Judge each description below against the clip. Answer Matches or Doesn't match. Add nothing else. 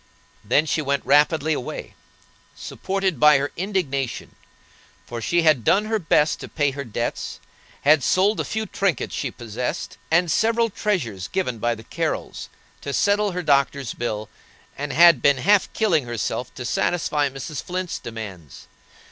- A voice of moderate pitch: Matches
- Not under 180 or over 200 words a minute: Doesn't match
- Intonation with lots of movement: Matches